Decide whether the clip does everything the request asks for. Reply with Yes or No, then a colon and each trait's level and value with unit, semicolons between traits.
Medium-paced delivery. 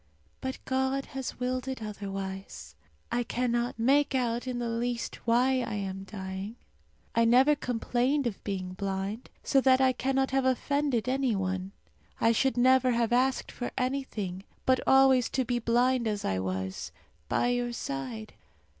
Yes: average, 155 wpm